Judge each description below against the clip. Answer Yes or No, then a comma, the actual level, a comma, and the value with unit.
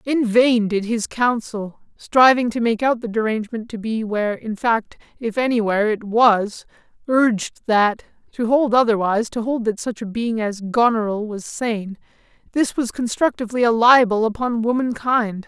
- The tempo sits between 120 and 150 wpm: No, average, 165 wpm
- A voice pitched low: No, high, 225 Hz